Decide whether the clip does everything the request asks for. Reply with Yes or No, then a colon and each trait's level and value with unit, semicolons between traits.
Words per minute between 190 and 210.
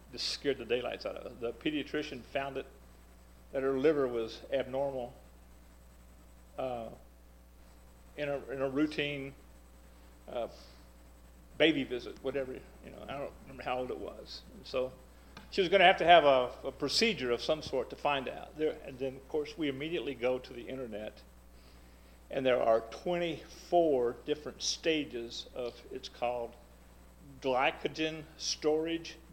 No: average, 155 wpm